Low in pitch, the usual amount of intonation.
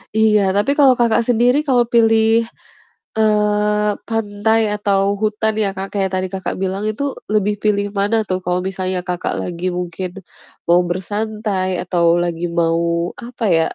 No: high, 205 Hz; average, 3.1 semitones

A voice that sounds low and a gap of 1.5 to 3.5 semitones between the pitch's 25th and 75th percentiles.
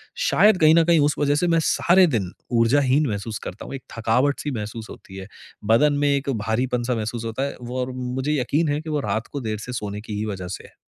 No: low, 125 Hz; average, 4.7 semitones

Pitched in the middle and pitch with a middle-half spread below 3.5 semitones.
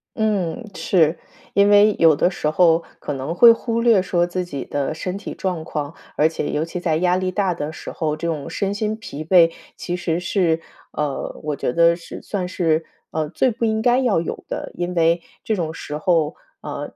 No: medium, 175 Hz; average, 3.8 semitones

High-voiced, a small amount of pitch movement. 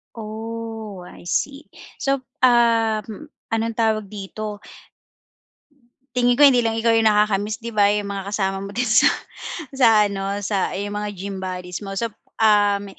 Yes: high, 215 Hz; narrow, 2.2 semitones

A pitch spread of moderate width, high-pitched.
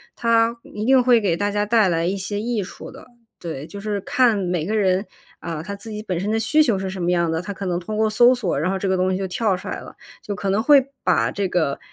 Yes: average, 3.4 semitones; high, 200 Hz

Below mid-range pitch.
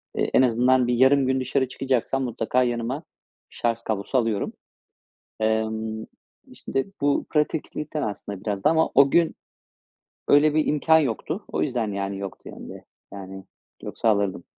Yes: low, 125 Hz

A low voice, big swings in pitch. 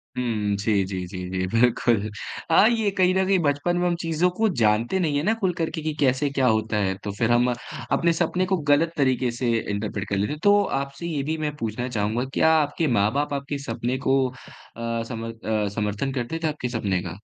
Yes: low, 130 Hz; wide, 6.7 semitones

